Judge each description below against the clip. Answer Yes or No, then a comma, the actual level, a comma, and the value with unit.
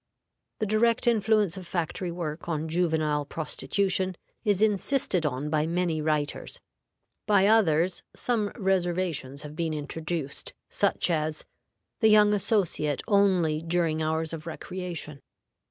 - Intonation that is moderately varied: Yes, average, 4.2 semitones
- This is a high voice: No, medium, 170 Hz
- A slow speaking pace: Yes, slow, 120 wpm